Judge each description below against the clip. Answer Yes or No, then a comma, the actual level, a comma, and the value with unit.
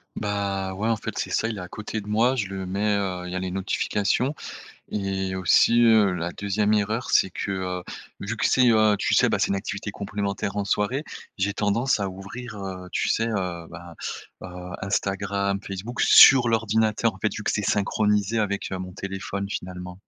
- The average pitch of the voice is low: Yes, low, 100 Hz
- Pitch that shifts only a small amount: Yes, narrow, 2.2 semitones